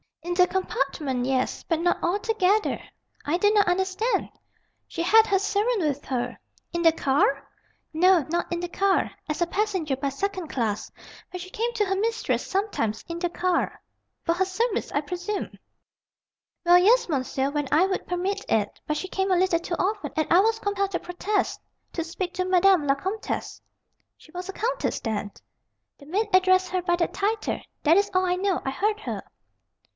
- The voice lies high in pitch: Yes, very high, 365 Hz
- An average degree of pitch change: Yes, average, 3.8 semitones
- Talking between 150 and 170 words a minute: No, average, 190 wpm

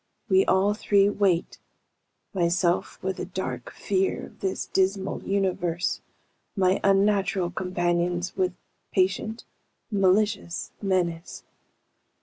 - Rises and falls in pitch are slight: Yes, narrow, 1.9 semitones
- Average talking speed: No, slow, 100 wpm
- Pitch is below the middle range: No, high, 190 Hz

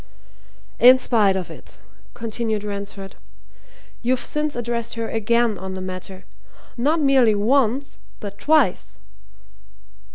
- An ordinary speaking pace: No, slow, 110 wpm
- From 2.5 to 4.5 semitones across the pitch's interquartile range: Yes, average, 4.0 semitones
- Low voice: No, high, 230 Hz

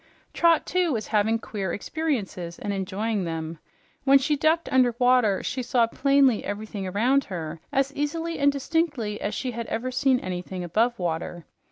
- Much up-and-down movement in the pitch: Yes, wide, 6.1 semitones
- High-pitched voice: Yes, high, 235 Hz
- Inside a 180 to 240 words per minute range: No, average, 165 wpm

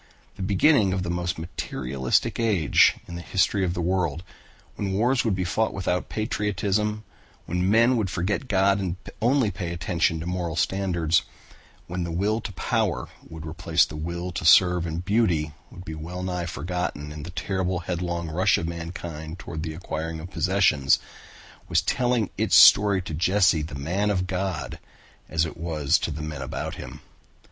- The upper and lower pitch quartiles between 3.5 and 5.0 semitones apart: No, average, 3.1 semitones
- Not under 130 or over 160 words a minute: No, average, 175 wpm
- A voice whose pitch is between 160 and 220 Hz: No, very low, 90 Hz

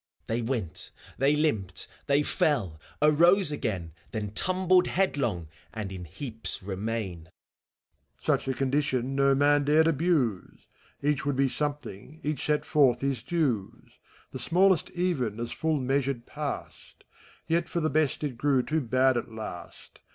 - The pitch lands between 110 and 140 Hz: Yes, low, 135 Hz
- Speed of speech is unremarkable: Yes, average, 150 wpm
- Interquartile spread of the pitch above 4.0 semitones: Yes, average, 5.2 semitones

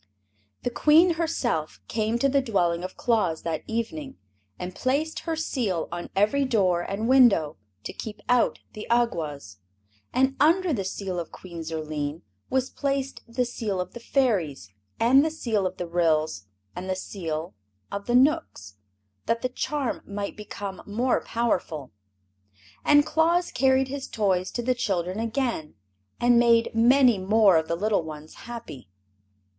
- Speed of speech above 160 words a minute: No, average, 155 wpm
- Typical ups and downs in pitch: No, wide, 6.9 semitones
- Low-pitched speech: No, high, 220 Hz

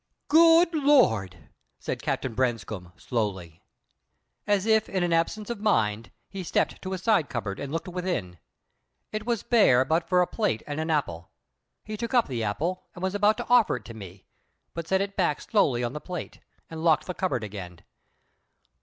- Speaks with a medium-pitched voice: Yes, medium, 165 Hz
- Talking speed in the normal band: Yes, average, 180 wpm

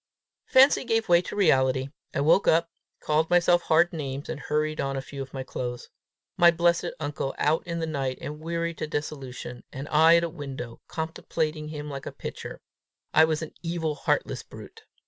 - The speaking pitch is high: No, medium, 155 Hz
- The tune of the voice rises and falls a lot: No, average, 3.3 semitones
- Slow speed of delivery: No, average, 185 wpm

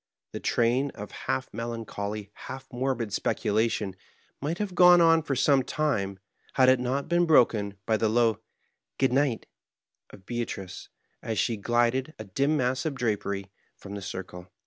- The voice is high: No, low, 120 Hz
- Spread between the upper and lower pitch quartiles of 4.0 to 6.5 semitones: Yes, average, 4.7 semitones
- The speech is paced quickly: No, average, 155 wpm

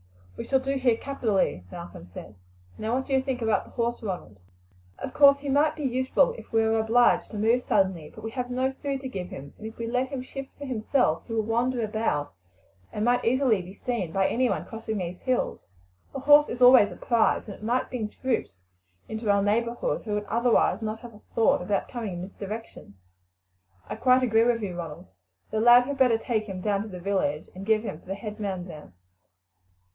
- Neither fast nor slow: No, fast, 220 wpm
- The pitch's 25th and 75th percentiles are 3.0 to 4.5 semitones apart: Yes, average, 4.2 semitones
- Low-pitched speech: No, high, 225 Hz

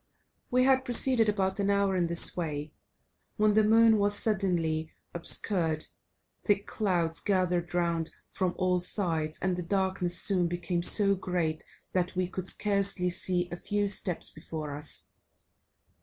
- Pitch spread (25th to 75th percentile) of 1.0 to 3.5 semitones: Yes, average, 2.9 semitones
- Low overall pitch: No, medium, 185 Hz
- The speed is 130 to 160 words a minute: Yes, average, 145 wpm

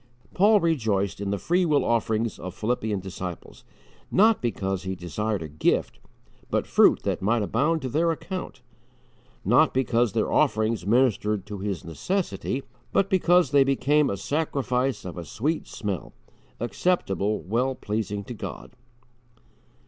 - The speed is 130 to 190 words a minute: Yes, average, 140 wpm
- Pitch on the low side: Yes, low, 115 Hz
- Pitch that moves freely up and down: Yes, wide, 6.7 semitones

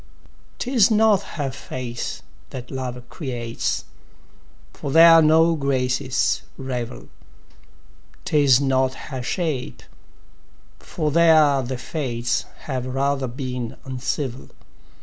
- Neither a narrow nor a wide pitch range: Yes, average, 3.4 semitones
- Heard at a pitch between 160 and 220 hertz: No, low, 135 Hz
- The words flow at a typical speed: No, slow, 95 wpm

